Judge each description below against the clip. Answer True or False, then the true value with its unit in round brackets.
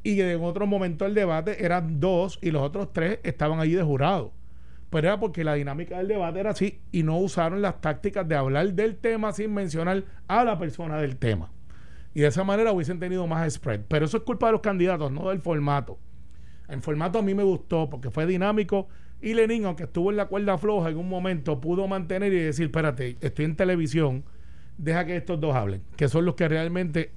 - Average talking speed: False (215 wpm)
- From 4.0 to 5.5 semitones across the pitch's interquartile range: True (4.3 semitones)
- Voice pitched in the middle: True (175 Hz)